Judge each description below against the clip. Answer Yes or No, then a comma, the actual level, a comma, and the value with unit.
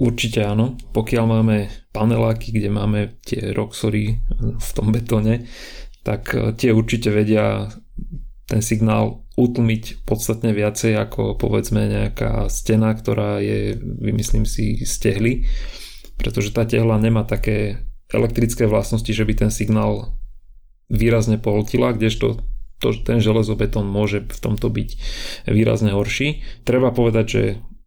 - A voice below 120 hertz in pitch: Yes, low, 110 Hz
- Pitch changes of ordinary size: No, narrow, 1.5 semitones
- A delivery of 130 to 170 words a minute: No, average, 120 wpm